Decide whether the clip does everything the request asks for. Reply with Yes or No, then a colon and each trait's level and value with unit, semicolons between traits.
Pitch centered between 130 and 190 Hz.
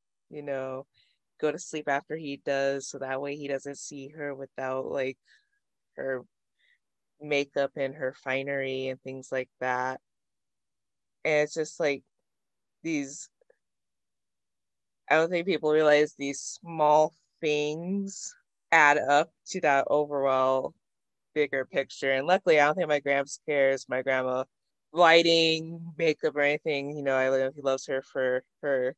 Yes: medium, 140 Hz